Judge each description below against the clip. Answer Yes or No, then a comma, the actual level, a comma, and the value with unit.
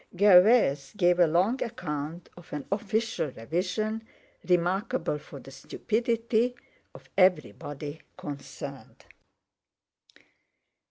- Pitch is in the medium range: Yes, medium, 180 Hz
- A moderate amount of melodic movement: No, wide, 6.5 semitones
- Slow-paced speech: Yes, slow, 90 wpm